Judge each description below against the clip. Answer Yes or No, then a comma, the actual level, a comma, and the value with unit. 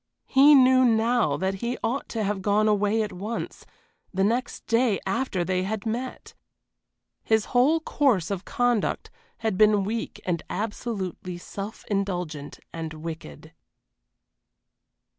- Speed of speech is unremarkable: No, slow, 130 wpm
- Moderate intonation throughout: Yes, average, 3.9 semitones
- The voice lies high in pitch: Yes, high, 210 Hz